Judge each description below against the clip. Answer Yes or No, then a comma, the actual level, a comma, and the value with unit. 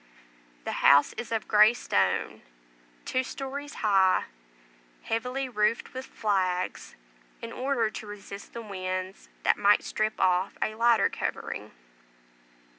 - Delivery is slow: Yes, slow, 120 wpm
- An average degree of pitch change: Yes, average, 3.9 semitones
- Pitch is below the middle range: No, high, 215 Hz